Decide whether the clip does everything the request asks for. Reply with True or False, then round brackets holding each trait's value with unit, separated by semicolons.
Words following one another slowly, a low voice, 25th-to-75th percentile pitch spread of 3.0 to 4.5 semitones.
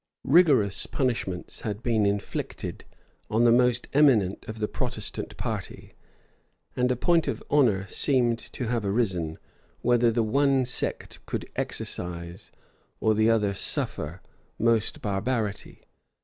True (125 wpm; 115 Hz; 3.7 semitones)